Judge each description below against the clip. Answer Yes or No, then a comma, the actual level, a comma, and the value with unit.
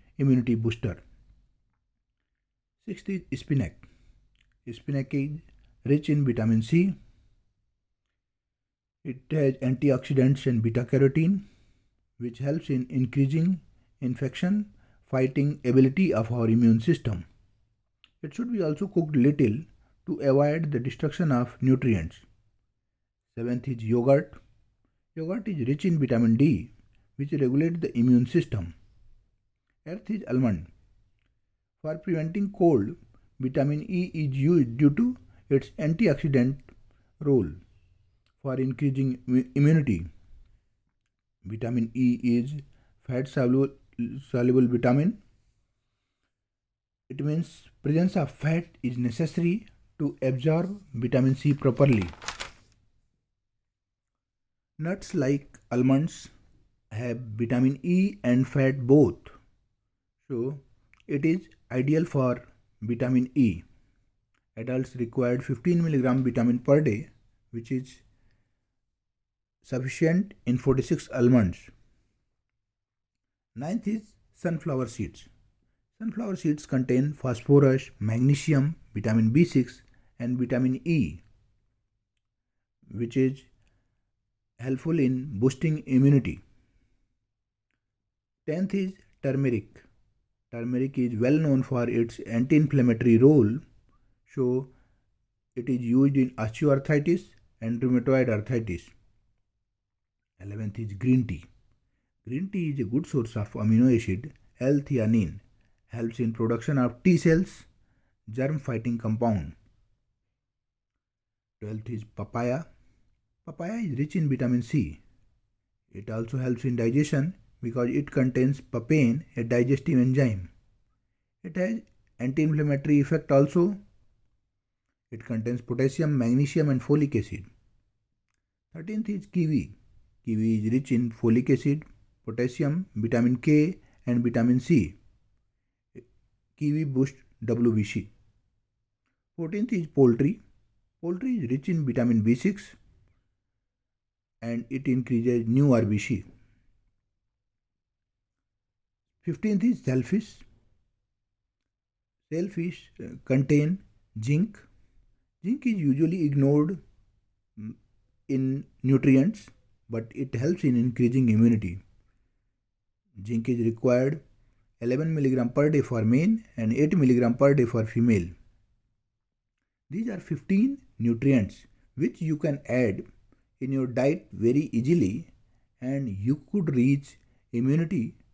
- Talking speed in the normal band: No, slow, 100 wpm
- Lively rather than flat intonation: No, average, 4.2 semitones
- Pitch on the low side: Yes, low, 120 Hz